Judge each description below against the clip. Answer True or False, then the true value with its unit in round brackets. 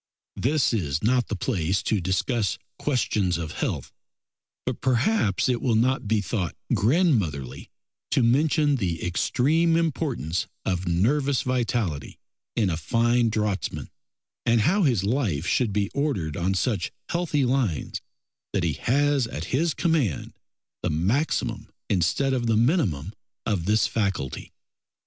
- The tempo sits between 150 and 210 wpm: False (135 wpm)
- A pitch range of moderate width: False (6.5 semitones)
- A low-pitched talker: True (115 Hz)